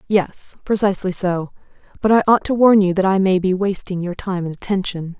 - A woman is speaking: Yes, female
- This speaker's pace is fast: Yes, fast, 210 wpm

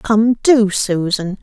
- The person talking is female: Yes, female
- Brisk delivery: No, slow, 125 wpm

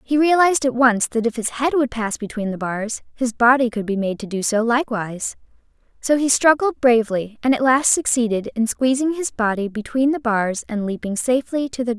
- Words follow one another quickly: Yes, fast, 215 wpm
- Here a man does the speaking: No, female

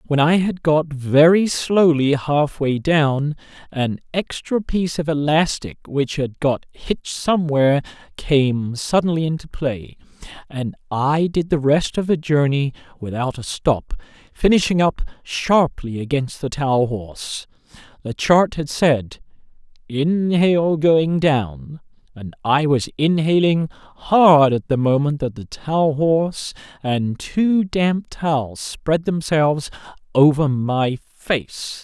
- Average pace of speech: No, slow, 130 wpm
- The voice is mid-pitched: Yes, medium, 150 Hz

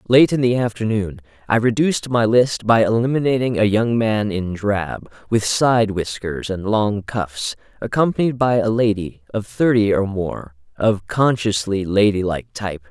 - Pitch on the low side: Yes, low, 110 Hz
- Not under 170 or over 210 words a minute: No, average, 155 wpm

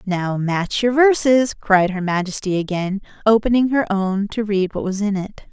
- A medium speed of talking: Yes, average, 185 wpm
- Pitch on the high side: Yes, high, 205 Hz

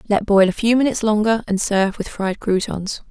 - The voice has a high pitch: Yes, high, 205 Hz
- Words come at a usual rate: No, fast, 215 wpm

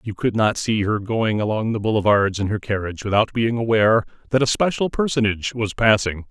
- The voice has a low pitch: Yes, low, 110 Hz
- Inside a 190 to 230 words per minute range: Yes, average, 200 wpm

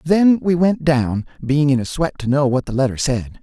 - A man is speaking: Yes, male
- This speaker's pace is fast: Yes, fast, 245 wpm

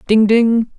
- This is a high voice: Yes, high, 225 Hz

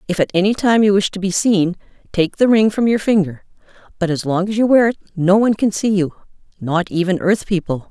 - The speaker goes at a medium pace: No, fast, 230 wpm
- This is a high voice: Yes, high, 195 Hz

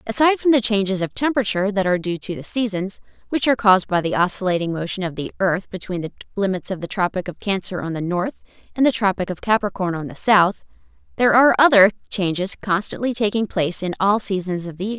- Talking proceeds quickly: Yes, fast, 215 wpm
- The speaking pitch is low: No, high, 200 Hz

